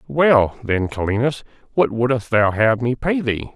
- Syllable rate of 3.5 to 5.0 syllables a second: Yes, 4.1 syllables/s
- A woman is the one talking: No, male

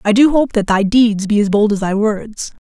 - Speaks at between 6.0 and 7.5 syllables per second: No, 4.9 syllables/s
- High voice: Yes, high, 215 Hz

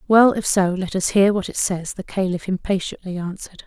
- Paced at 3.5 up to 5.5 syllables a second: Yes, 5.4 syllables/s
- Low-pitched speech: No, high, 190 Hz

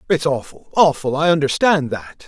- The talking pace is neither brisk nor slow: Yes, average, 160 wpm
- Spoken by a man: Yes, male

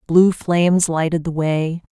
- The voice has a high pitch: No, medium, 165 Hz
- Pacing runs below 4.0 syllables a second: No, 4.1 syllables/s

